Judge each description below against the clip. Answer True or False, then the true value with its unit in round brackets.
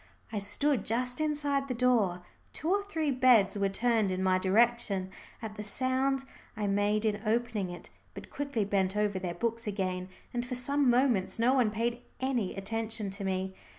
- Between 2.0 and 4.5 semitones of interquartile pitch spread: True (4.2 semitones)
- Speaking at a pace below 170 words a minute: False (180 wpm)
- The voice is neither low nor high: False (225 Hz)